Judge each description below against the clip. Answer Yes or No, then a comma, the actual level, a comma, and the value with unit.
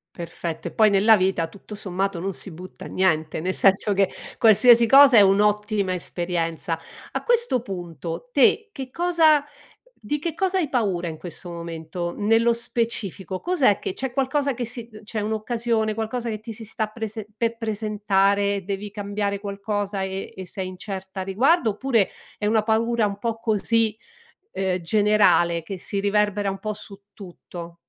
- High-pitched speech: Yes, high, 210 Hz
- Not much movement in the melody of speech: No, average, 3.3 semitones